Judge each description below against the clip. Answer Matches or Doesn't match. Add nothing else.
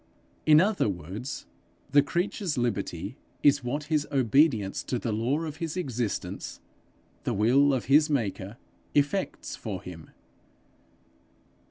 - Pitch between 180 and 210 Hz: Doesn't match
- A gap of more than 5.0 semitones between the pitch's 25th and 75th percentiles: Matches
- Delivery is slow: Matches